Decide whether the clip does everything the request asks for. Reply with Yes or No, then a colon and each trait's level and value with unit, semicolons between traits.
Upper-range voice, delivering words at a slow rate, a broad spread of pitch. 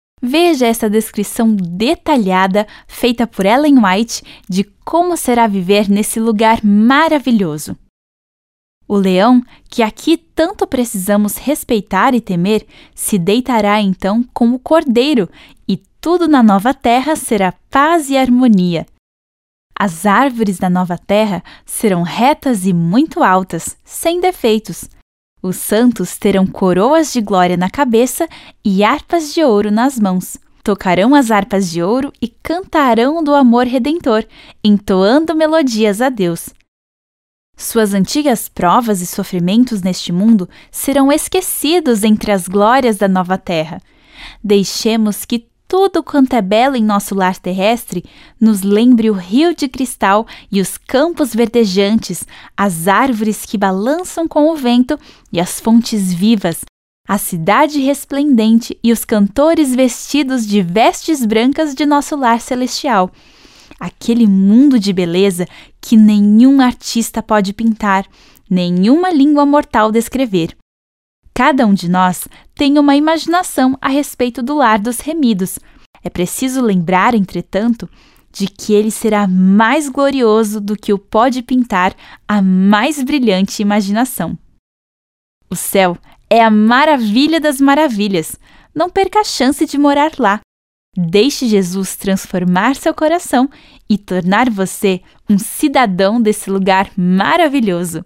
No: high, 225 Hz; average, 130 wpm; wide, 6.0 semitones